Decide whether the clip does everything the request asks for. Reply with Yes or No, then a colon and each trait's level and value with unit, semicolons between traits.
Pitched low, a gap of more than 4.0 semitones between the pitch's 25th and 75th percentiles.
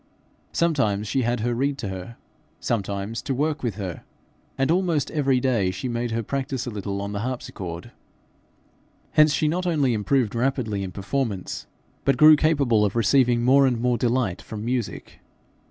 Yes: low, 120 Hz; average, 4.8 semitones